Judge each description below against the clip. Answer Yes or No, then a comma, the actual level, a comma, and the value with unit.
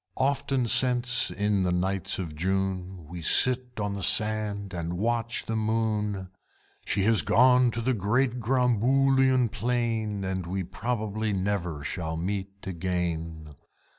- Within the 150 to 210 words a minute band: No, slow, 135 wpm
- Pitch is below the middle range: Yes, low, 105 Hz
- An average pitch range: Yes, average, 4.2 semitones